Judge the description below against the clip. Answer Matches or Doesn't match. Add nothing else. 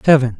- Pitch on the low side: Matches